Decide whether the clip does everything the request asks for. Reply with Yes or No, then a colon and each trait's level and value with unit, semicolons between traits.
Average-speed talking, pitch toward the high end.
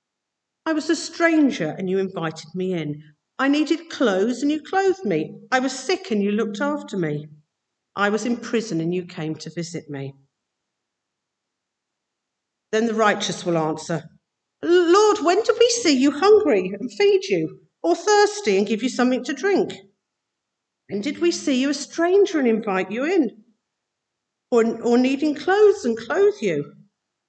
Yes: average, 165 wpm; high, 235 Hz